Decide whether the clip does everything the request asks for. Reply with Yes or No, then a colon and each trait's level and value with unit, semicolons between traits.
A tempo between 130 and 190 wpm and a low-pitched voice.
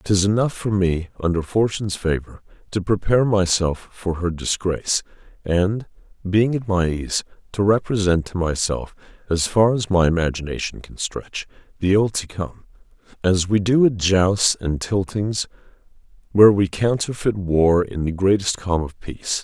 Yes: average, 155 wpm; very low, 95 Hz